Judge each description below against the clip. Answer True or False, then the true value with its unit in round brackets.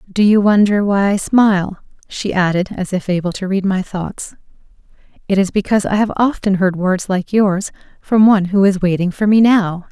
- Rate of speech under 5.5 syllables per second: True (5.1 syllables/s)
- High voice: True (195 Hz)